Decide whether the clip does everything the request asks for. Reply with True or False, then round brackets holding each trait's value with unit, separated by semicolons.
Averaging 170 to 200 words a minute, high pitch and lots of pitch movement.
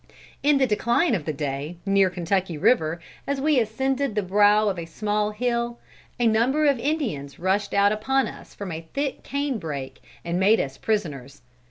True (175 wpm; 210 Hz; 6.6 semitones)